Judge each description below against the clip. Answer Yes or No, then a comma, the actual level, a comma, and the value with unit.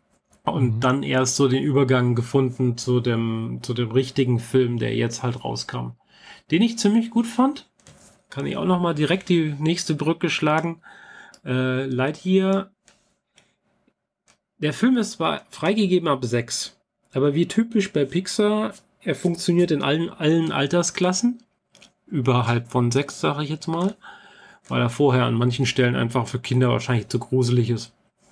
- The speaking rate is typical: Yes, average, 155 wpm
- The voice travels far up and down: Yes, wide, 6.5 semitones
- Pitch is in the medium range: Yes, medium, 145 Hz